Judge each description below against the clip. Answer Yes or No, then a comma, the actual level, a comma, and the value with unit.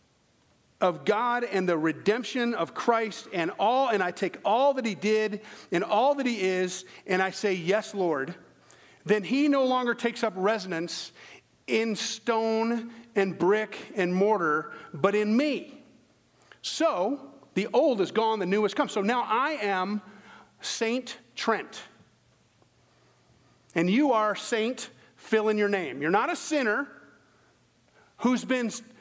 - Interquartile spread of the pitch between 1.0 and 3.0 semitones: No, average, 3.8 semitones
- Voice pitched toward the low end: No, high, 215 Hz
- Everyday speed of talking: Yes, average, 145 wpm